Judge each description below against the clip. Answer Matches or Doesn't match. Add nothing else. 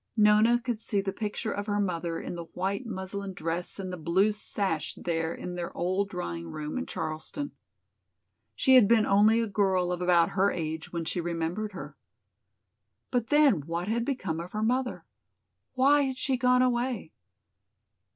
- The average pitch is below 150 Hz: Doesn't match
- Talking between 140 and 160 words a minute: Doesn't match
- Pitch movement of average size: Matches